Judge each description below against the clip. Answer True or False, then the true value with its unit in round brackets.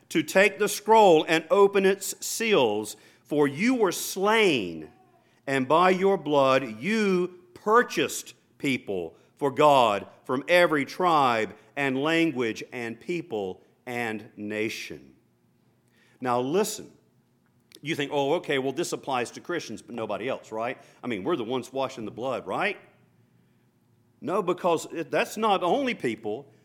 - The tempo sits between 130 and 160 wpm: True (135 wpm)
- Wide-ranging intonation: True (7.1 semitones)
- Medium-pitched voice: True (150 Hz)